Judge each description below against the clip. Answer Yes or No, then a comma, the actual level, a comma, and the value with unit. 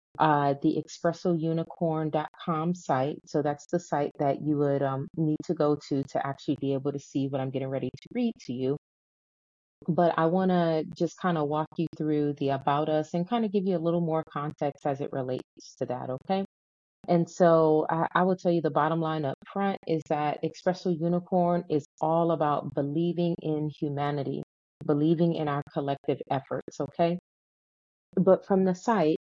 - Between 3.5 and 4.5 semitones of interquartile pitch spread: No, average, 3.0 semitones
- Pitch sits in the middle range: Yes, medium, 155 Hz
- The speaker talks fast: No, average, 185 wpm